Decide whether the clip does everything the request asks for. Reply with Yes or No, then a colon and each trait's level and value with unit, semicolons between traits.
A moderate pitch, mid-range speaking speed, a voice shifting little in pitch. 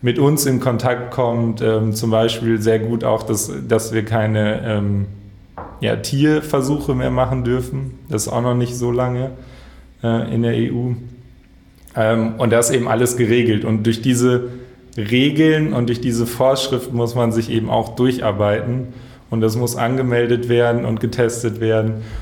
No: low, 120 Hz; average, 160 wpm; narrow, 2.1 semitones